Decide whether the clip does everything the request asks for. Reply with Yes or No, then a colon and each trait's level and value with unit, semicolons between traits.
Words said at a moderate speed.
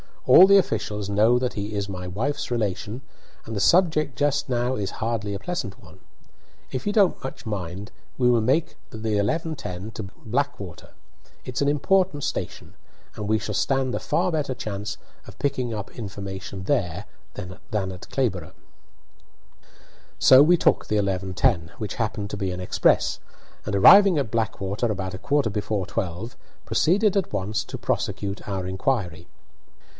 Yes: average, 160 wpm